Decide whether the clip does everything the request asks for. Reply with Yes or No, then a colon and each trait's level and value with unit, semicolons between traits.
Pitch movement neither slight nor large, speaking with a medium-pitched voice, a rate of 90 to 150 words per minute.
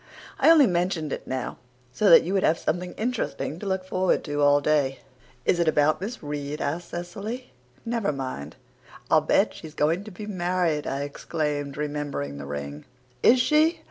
No: average, 4.9 semitones; medium, 160 Hz; average, 175 wpm